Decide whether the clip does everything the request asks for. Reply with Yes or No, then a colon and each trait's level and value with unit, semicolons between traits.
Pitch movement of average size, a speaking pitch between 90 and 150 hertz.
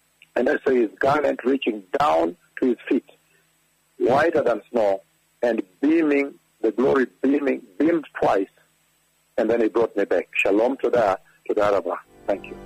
No: wide, 6.7 semitones; medium, 140 Hz